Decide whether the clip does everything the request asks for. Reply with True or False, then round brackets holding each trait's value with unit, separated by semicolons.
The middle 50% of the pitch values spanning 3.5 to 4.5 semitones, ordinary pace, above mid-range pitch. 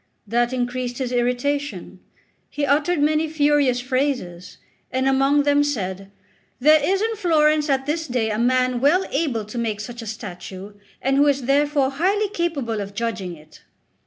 True (3.9 semitones; 160 wpm; 265 Hz)